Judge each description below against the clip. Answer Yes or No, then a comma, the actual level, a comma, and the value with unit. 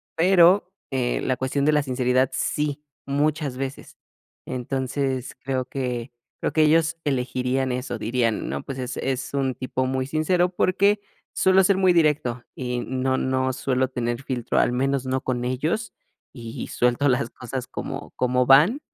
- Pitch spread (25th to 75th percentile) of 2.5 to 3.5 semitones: Yes, average, 2.9 semitones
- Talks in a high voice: No, low, 130 Hz